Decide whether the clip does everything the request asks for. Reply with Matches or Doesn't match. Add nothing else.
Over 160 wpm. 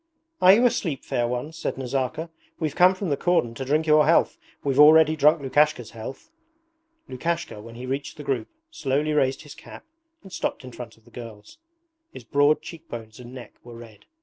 Matches